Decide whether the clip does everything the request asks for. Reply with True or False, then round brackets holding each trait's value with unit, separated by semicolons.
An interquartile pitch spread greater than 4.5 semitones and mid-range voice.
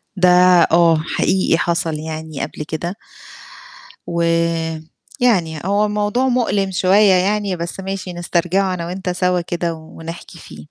False (2.6 semitones; 180 Hz)